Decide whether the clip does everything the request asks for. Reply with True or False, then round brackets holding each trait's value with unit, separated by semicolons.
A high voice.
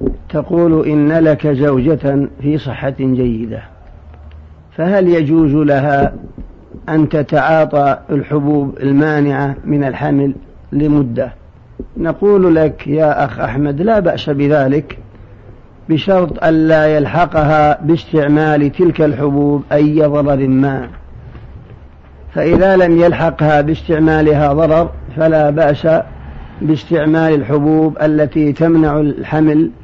False (150 Hz)